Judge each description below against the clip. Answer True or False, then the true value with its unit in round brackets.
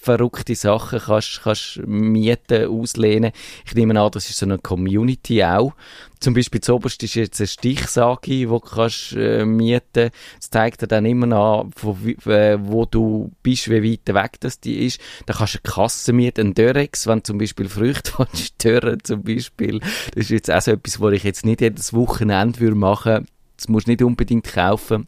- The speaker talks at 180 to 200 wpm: True (185 wpm)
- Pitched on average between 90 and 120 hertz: True (115 Hz)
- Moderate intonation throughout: False (2.1 semitones)